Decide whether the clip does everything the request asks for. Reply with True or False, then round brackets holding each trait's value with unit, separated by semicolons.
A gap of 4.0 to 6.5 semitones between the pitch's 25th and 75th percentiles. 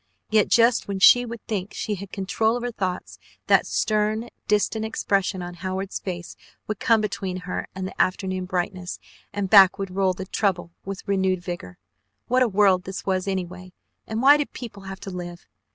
False (2.6 semitones)